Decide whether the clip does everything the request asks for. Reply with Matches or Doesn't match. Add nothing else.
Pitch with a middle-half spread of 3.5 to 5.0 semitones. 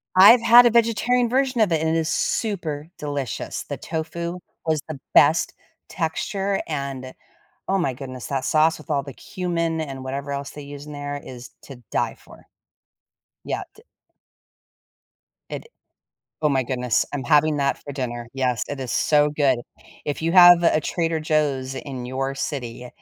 Matches